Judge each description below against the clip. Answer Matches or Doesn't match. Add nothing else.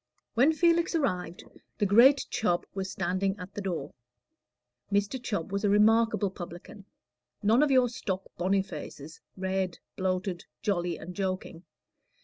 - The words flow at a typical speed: Doesn't match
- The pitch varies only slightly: Doesn't match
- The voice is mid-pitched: Doesn't match